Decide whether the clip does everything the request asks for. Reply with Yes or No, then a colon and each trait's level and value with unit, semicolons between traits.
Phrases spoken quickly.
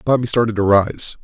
No: average, 195 wpm